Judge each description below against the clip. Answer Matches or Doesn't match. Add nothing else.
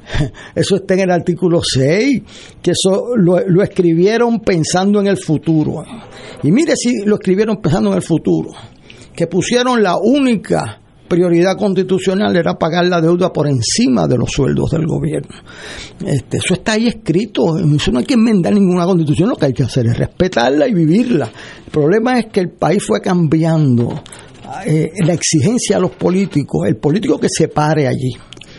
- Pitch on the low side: Doesn't match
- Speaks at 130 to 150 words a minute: Doesn't match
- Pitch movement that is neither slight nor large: Matches